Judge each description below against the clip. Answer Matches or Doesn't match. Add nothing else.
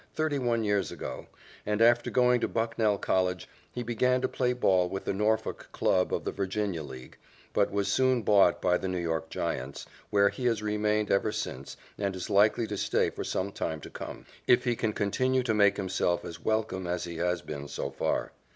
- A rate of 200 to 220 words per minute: Matches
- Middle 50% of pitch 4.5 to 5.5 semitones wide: Doesn't match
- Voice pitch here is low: Matches